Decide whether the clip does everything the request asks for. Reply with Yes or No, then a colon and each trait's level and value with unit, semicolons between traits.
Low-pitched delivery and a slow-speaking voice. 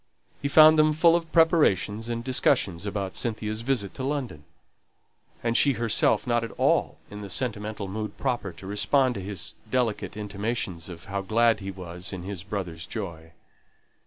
No: low, 105 Hz; average, 165 wpm